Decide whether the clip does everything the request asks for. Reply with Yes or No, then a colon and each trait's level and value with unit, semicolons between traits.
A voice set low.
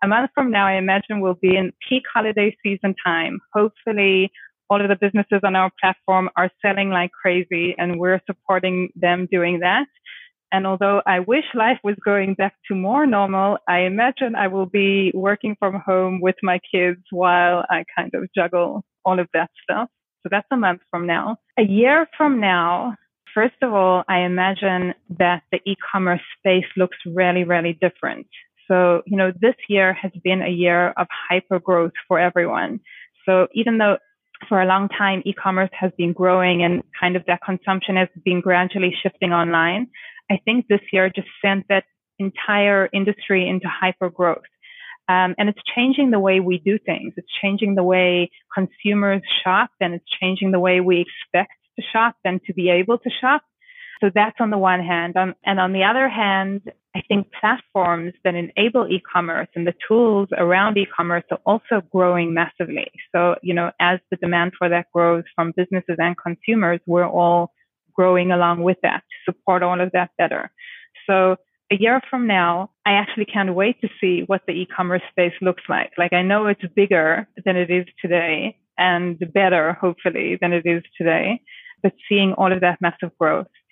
No: high, 190 Hz